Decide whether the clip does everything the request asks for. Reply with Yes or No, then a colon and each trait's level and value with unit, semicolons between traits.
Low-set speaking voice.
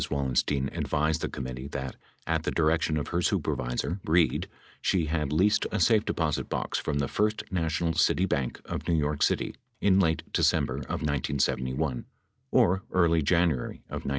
Yes: very low, 80 Hz